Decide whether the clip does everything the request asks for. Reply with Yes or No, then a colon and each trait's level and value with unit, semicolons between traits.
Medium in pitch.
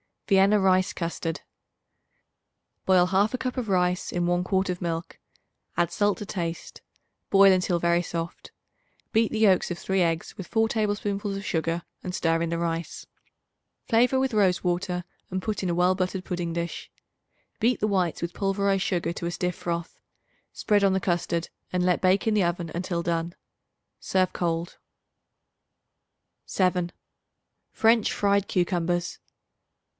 Yes: medium, 180 Hz